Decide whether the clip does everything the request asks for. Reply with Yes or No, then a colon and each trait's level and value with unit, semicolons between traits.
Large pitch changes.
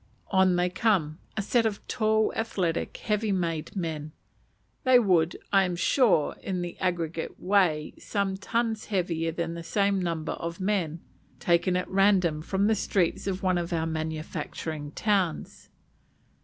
No: average, 3.4 semitones